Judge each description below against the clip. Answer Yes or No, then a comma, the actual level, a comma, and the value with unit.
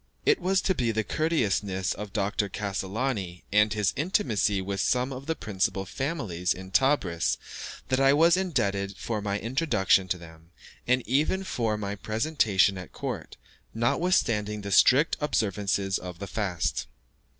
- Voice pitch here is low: Yes, low, 105 Hz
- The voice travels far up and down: Yes, wide, 5.7 semitones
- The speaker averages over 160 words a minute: No, average, 145 wpm